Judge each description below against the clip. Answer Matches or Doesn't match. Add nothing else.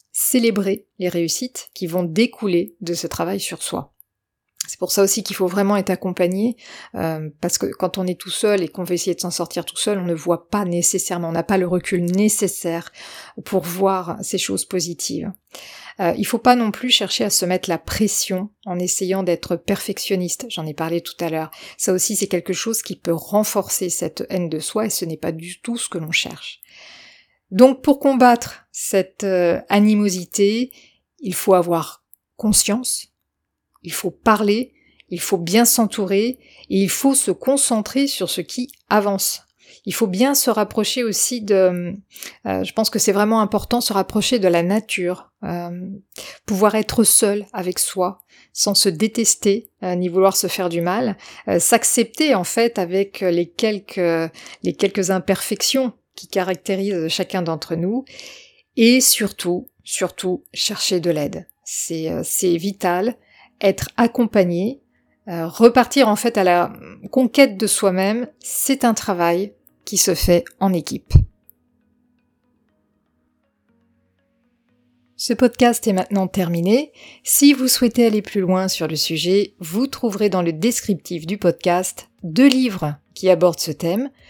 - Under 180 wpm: Matches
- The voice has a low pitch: Doesn't match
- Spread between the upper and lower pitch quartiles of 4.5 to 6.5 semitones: Doesn't match